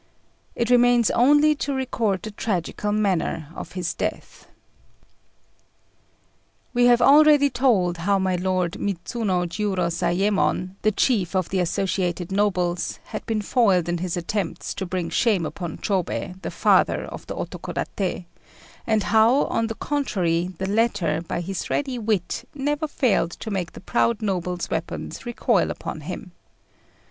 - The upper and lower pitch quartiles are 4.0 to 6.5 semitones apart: Yes, average, 4.7 semitones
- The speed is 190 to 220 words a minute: No, average, 140 wpm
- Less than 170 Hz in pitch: No, high, 195 Hz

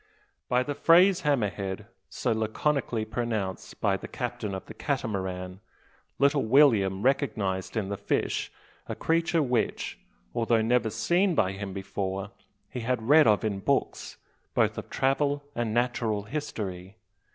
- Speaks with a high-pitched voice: No, low, 115 Hz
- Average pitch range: No, wide, 5.9 semitones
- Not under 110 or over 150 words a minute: Yes, average, 140 wpm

